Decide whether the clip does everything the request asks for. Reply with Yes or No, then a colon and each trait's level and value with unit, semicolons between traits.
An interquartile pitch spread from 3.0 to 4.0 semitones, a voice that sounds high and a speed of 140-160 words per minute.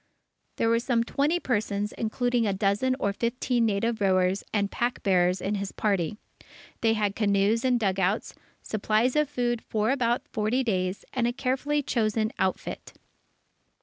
Yes: average, 3.5 semitones; high, 220 Hz; average, 150 wpm